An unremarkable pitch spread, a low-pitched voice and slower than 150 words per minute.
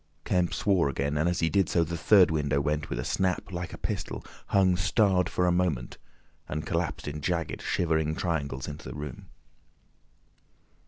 No: average, 3.3 semitones; very low, 85 Hz; average, 175 wpm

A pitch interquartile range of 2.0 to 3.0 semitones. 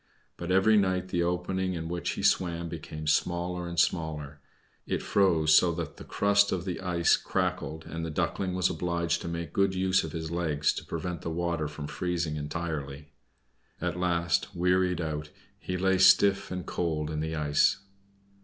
Yes: narrow, 2.5 semitones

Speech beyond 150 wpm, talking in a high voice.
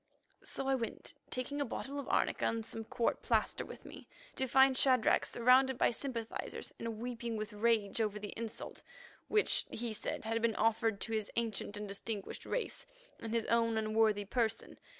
Yes: average, 175 wpm; high, 230 Hz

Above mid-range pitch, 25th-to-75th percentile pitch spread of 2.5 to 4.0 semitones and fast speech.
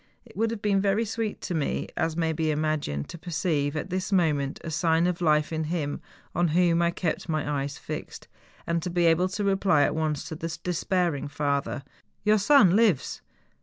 No: medium, 165 Hz; average, 3.4 semitones; fast, 215 wpm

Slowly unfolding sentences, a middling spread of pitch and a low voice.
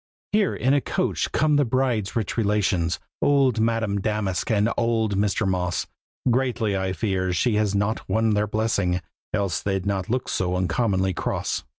No: average, 165 wpm; average, 3.3 semitones; low, 105 Hz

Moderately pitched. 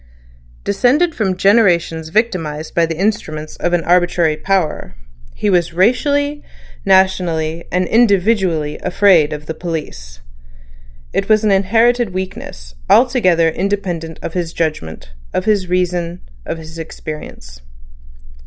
Yes: medium, 180 Hz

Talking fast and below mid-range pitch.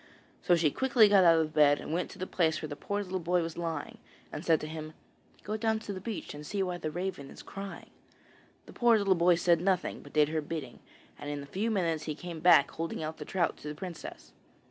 No: fast, 245 wpm; medium, 170 Hz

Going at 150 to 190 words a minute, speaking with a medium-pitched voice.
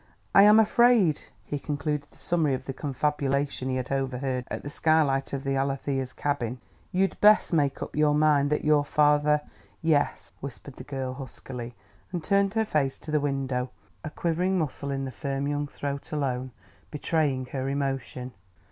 Yes: average, 175 wpm; medium, 145 Hz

